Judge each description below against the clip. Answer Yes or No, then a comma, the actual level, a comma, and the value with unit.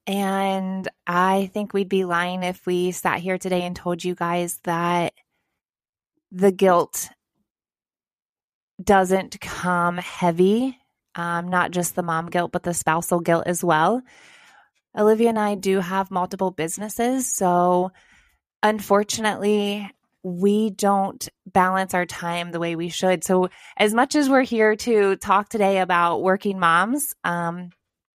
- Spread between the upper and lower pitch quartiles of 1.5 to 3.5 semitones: Yes, narrow, 2.6 semitones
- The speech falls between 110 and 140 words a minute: Yes, slow, 135 wpm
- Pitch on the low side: No, medium, 185 Hz